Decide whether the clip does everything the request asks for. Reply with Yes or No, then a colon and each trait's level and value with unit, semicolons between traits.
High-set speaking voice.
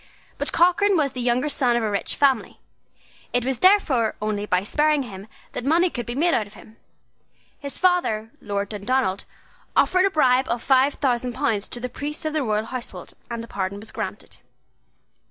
Yes: very high, 250 Hz